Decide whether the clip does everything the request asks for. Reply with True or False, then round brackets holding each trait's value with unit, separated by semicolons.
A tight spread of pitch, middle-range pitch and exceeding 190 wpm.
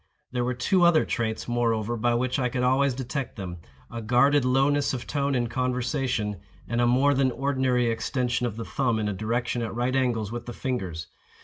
False (2.1 semitones; 125 Hz; 200 wpm)